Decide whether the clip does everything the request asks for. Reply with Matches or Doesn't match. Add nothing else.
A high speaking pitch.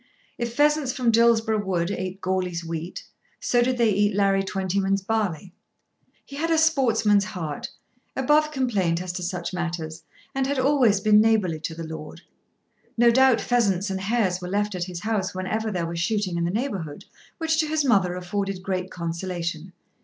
Matches